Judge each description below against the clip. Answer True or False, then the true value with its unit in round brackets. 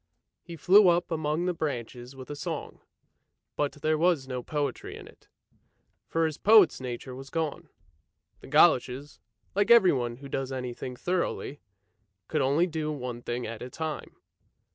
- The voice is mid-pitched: True (145 Hz)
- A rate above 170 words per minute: False (160 wpm)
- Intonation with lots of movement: False (4.3 semitones)